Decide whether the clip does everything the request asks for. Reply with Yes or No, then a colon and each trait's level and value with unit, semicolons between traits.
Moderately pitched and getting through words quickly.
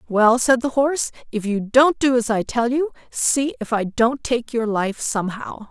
No: high, 240 Hz; fast, 210 wpm